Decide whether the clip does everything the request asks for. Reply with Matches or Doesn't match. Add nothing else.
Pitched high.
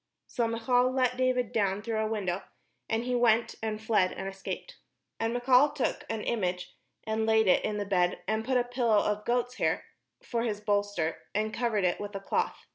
Matches